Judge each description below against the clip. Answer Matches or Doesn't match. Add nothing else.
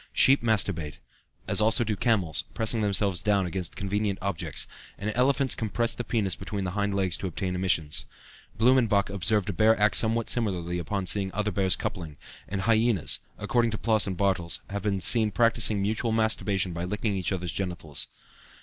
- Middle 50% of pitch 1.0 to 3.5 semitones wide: Matches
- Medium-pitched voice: Doesn't match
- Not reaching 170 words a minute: Doesn't match